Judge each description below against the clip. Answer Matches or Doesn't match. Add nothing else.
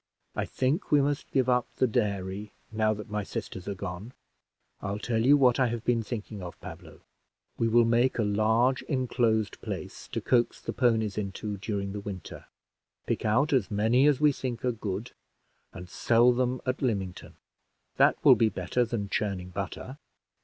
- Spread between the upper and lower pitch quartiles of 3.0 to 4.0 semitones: Matches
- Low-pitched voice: Matches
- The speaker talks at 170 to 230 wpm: Matches